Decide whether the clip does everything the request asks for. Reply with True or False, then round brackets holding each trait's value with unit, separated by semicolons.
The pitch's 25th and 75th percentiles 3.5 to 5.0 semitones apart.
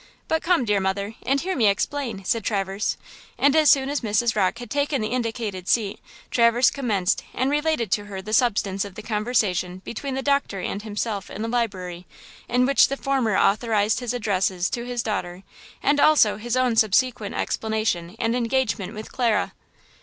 True (4.1 semitones)